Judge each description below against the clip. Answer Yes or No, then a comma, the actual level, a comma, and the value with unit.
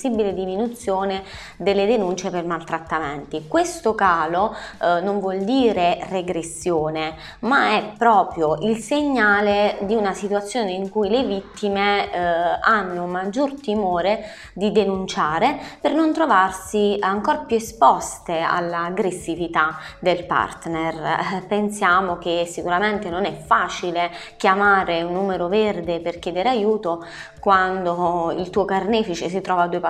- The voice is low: No, high, 190 Hz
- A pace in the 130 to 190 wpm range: No, average, 120 wpm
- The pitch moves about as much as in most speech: Yes, average, 3.4 semitones